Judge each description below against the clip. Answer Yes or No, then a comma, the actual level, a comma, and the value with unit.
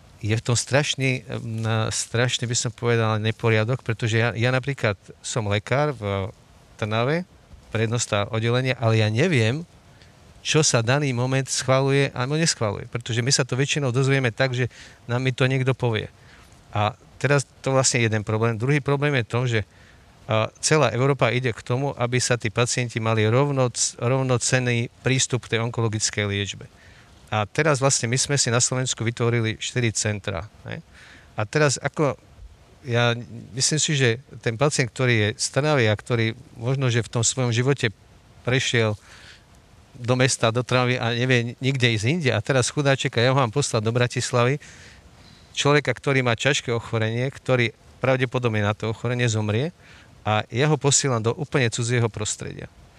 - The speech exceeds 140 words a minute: Yes, average, 155 wpm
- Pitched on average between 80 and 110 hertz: No, low, 120 Hz